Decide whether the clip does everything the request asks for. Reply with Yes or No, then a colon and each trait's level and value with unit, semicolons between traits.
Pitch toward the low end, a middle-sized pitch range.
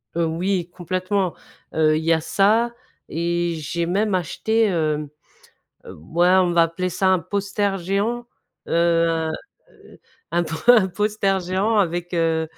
No: medium, 175 Hz; average, 3.0 semitones